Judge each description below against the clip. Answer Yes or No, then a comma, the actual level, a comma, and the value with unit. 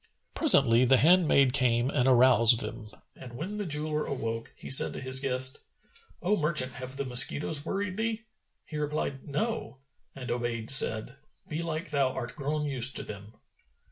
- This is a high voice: No, low, 135 Hz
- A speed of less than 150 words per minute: No, average, 160 wpm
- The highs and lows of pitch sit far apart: No, average, 3.6 semitones